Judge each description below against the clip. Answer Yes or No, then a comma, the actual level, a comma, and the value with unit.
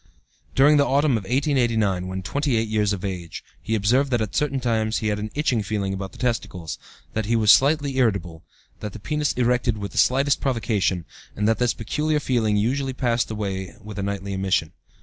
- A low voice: Yes, low, 110 Hz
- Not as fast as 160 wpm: No, average, 195 wpm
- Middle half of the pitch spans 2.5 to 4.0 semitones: No, average, 4.6 semitones